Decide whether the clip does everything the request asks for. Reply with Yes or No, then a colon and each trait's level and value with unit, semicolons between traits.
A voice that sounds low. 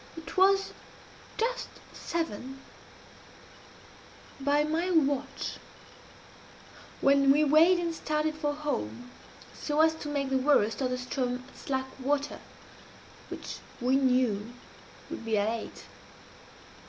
No: very high, 280 Hz